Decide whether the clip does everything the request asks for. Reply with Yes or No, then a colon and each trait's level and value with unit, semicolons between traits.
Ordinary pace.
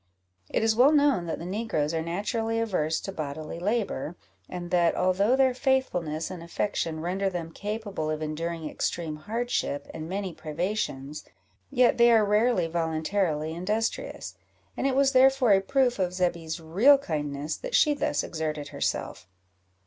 Yes: average, 155 wpm